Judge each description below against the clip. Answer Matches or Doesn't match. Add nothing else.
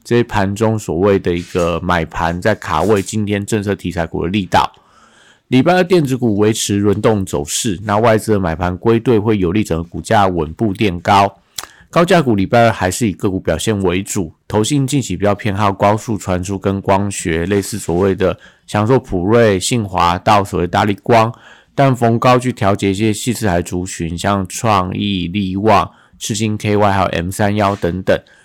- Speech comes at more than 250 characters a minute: Matches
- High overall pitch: Doesn't match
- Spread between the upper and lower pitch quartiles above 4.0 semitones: Doesn't match